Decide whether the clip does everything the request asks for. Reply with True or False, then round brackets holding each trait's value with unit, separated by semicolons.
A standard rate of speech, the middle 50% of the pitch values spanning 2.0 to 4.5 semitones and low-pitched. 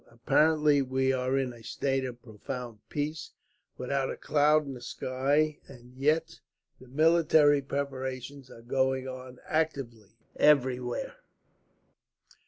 False (120 wpm; 2.5 semitones; 130 Hz)